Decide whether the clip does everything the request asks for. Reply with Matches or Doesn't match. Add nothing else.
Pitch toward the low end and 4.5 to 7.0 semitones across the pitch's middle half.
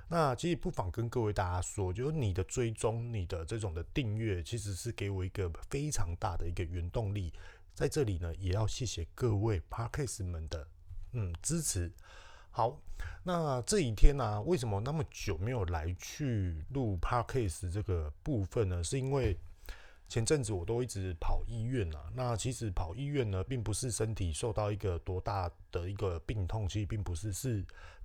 Matches